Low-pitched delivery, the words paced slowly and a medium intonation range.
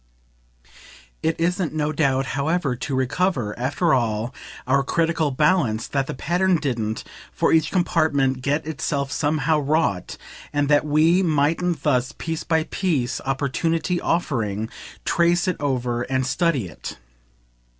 No: medium, 145 Hz; slow, 130 wpm; average, 4.1 semitones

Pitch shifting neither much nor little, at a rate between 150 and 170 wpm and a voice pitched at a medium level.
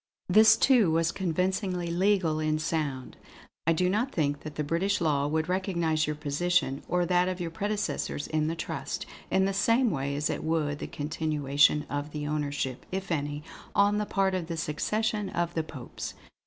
No: average, 4.1 semitones; average, 180 wpm; medium, 165 Hz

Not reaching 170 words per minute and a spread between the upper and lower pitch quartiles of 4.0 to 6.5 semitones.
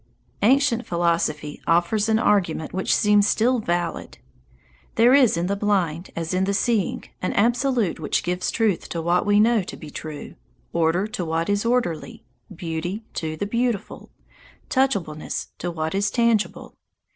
Yes: average, 155 wpm; average, 4.9 semitones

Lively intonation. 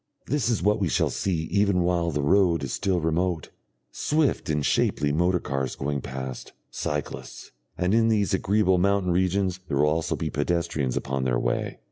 No: average, 4.8 semitones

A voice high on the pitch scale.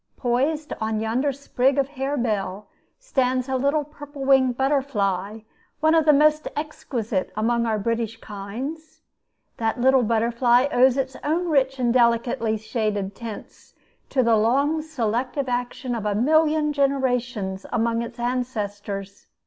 Yes: very high, 250 Hz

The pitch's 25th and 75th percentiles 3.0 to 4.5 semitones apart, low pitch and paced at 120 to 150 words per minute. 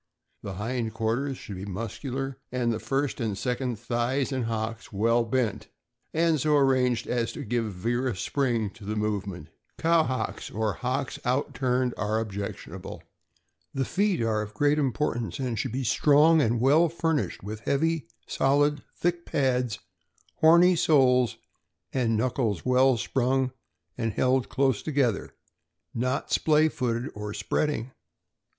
Yes: average, 3.6 semitones; low, 125 Hz; average, 145 wpm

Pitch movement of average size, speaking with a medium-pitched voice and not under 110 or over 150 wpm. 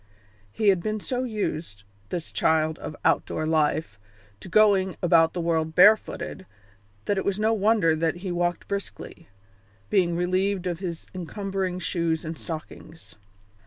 Yes: average, 3.4 semitones; medium, 175 Hz; average, 145 wpm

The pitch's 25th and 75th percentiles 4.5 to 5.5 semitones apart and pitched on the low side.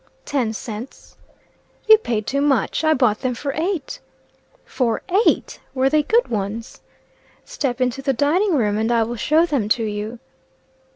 No: average, 4.8 semitones; very high, 255 Hz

